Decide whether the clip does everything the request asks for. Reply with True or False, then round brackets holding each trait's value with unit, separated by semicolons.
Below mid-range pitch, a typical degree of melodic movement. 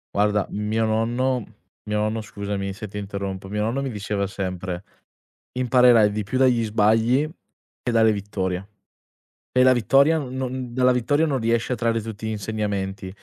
True (110 Hz; 3.5 semitones)